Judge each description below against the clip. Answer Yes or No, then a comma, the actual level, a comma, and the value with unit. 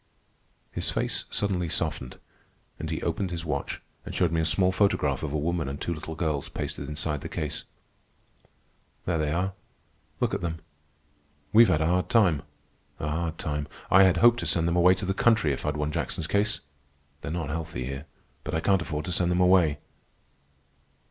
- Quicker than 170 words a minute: Yes, average, 190 wpm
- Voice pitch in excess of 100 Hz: No, very low, 80 Hz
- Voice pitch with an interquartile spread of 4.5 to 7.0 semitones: No, average, 3.2 semitones